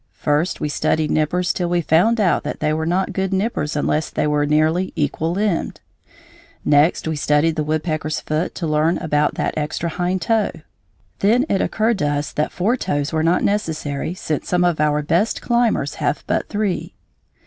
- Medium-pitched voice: Yes, medium, 160 Hz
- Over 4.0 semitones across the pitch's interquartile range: No, average, 3.7 semitones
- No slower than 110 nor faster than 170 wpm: No, average, 180 wpm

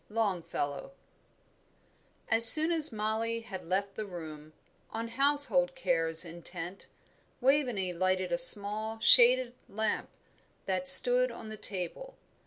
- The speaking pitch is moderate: No, high, 215 Hz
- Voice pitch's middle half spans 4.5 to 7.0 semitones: Yes, average, 5.2 semitones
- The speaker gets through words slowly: Yes, slow, 115 wpm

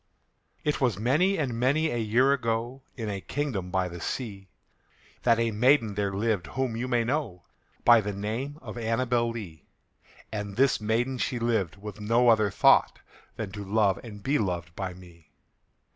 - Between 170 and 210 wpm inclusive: Yes, average, 175 wpm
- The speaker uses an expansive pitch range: No, average, 3.8 semitones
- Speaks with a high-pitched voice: No, low, 115 Hz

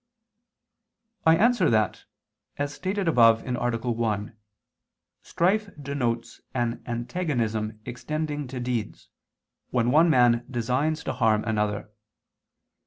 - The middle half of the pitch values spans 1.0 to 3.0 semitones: No, average, 4.9 semitones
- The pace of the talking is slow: Yes, slow, 105 wpm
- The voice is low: Yes, low, 125 Hz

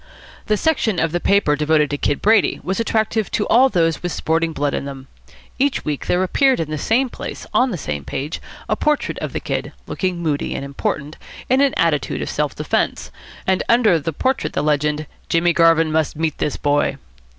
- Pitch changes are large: Yes, wide, 6.3 semitones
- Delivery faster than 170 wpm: Yes, average, 200 wpm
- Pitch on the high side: No, medium, 165 Hz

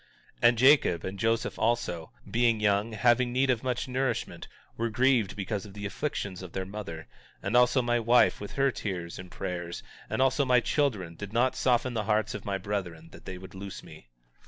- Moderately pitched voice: No, low, 110 Hz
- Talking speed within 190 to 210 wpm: Yes, average, 200 wpm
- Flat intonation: No, average, 4.3 semitones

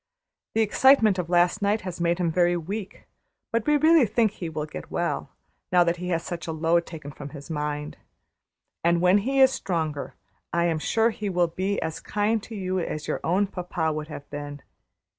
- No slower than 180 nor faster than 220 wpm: Yes, average, 200 wpm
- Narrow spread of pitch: No, average, 4.3 semitones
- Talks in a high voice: No, medium, 175 Hz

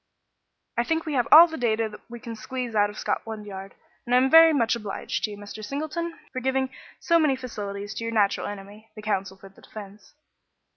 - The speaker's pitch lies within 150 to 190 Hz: No, high, 225 Hz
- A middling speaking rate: No, fast, 215 wpm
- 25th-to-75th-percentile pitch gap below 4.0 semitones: No, average, 4.3 semitones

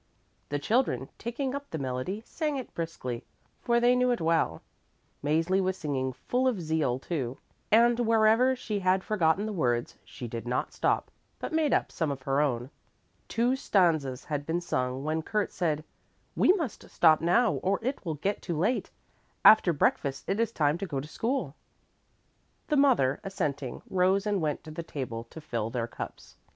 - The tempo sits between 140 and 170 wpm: No, average, 180 wpm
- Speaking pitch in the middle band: Yes, medium, 170 Hz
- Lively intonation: Yes, wide, 8.1 semitones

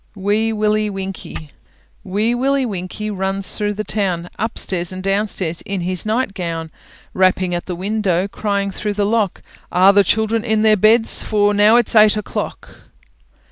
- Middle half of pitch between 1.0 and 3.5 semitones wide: Yes, narrow, 2.4 semitones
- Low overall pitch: No, high, 205 Hz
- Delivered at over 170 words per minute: No, average, 155 wpm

